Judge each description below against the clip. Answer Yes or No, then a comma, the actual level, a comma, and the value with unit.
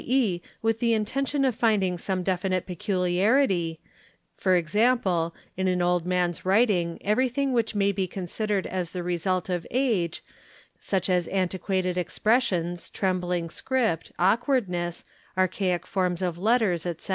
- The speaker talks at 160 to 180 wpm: No, slow, 135 wpm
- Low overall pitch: No, medium, 185 Hz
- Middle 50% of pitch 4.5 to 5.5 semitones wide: No, average, 3.7 semitones